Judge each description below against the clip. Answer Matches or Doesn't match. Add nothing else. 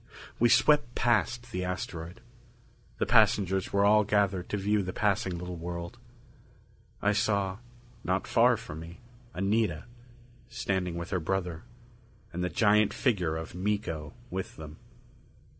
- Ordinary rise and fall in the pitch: Matches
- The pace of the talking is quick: Doesn't match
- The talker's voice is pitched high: Doesn't match